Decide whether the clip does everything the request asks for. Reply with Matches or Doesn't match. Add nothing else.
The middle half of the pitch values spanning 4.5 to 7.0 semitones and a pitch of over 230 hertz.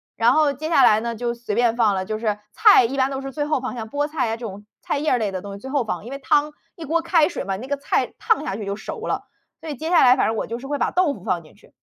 Matches